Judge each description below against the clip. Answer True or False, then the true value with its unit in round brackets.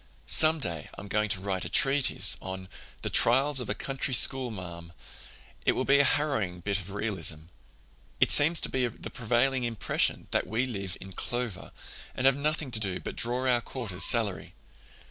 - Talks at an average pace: True (180 wpm)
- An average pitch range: False (5.7 semitones)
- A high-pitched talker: False (115 Hz)